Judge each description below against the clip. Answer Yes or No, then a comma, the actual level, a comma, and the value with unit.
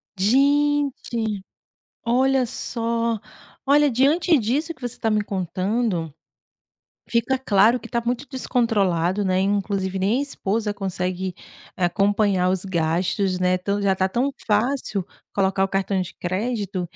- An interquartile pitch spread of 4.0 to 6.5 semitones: Yes, average, 4.5 semitones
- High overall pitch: Yes, high, 205 Hz